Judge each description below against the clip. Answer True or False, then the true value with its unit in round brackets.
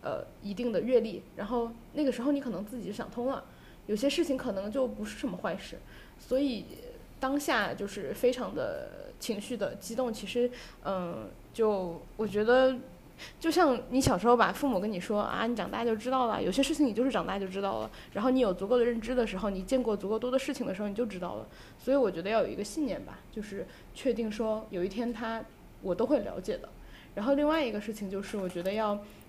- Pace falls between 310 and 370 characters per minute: True (325 characters per minute)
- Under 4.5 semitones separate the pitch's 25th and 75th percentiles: True (4.0 semitones)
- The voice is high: True (235 Hz)